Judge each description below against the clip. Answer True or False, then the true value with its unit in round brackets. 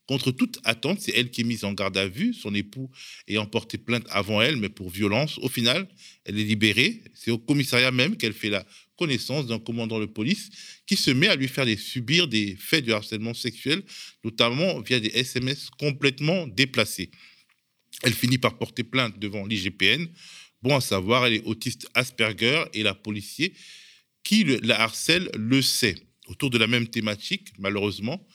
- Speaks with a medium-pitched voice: False (120 Hz)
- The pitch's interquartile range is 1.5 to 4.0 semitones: False (4.4 semitones)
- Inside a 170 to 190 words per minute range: True (180 wpm)